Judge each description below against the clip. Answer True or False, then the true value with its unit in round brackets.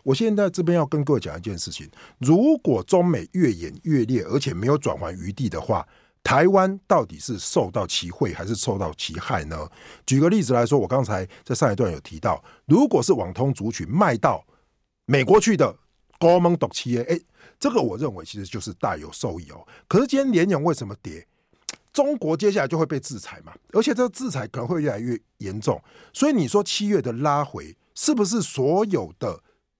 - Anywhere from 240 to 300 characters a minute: True (290 characters per minute)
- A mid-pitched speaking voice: True (145 Hz)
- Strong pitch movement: True (8.7 semitones)